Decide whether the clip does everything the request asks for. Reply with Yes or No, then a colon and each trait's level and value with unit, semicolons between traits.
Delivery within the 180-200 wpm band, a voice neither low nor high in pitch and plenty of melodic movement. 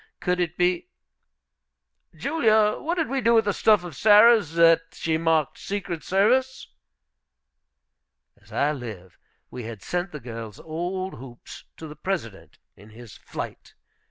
No: average, 145 wpm; medium, 170 Hz; wide, 8.4 semitones